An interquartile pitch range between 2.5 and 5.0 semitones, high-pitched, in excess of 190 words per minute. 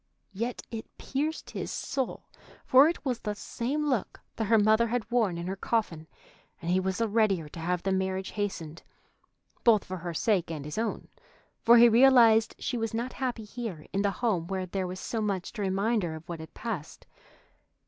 Yes: average, 4.2 semitones; high, 210 Hz; average, 200 wpm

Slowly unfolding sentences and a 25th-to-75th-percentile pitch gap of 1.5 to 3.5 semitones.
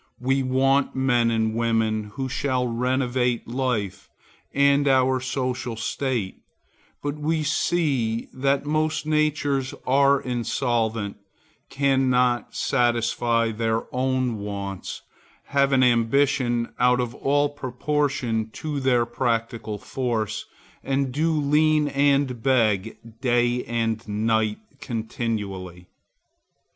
Yes: slow, 105 wpm; average, 3.2 semitones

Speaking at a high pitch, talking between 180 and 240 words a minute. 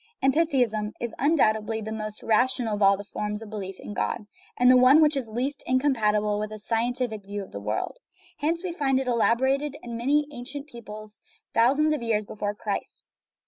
Yes: high, 235 Hz; average, 185 wpm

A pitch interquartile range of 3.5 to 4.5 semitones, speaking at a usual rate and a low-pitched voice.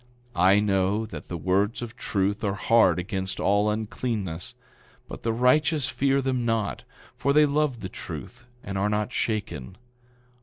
Yes: average, 3.9 semitones; average, 155 wpm; low, 105 Hz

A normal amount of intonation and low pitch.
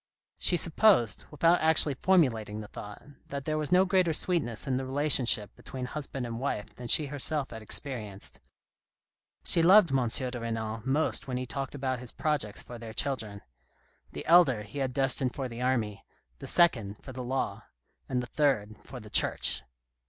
Yes: average, 4.6 semitones; low, 130 Hz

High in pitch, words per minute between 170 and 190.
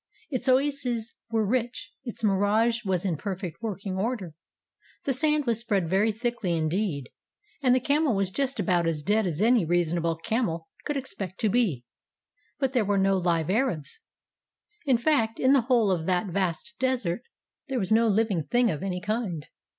Yes: high, 215 Hz; average, 175 wpm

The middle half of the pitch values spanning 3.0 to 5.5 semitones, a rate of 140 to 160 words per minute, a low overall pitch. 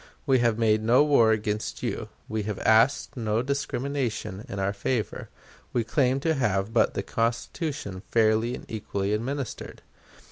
Yes: average, 3.5 semitones; average, 150 wpm; low, 115 Hz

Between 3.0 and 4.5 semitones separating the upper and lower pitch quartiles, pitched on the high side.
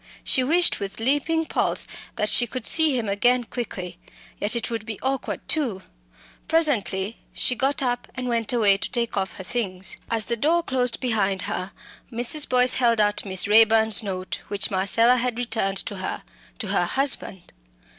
Yes: average, 4.1 semitones; high, 230 Hz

